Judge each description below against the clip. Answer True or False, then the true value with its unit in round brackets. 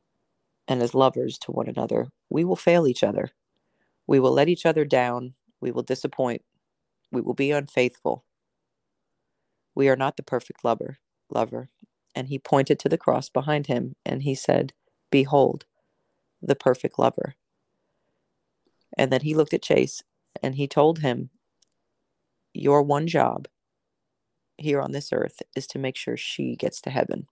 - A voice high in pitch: False (135 Hz)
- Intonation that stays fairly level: True (2.1 semitones)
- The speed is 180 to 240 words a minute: False (155 wpm)